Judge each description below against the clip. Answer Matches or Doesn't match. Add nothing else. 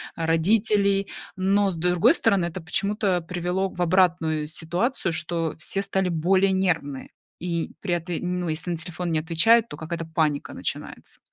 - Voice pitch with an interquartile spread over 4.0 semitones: Doesn't match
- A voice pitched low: Doesn't match